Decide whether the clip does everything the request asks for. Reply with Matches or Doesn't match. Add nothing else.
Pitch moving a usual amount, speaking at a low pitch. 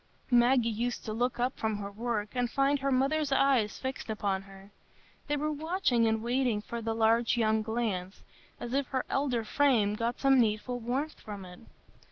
Doesn't match